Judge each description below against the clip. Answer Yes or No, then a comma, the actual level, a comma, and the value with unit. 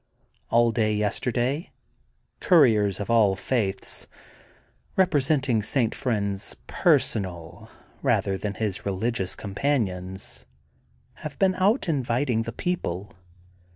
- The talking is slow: Yes, slow, 105 wpm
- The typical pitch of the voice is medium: No, low, 115 Hz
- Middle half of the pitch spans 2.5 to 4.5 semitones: No, average, 5.2 semitones